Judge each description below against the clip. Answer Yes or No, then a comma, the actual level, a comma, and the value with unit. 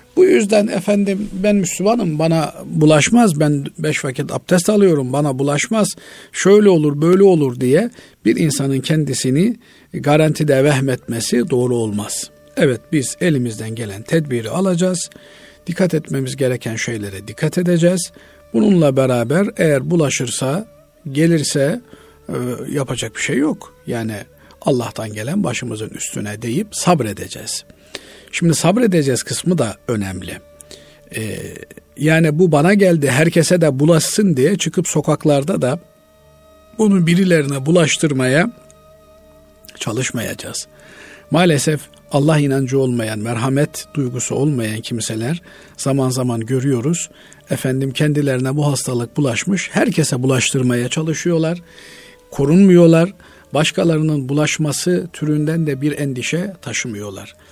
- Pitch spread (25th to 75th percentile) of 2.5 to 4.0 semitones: No, average, 5.3 semitones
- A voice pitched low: No, medium, 150 Hz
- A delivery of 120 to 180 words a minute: No, average, 105 wpm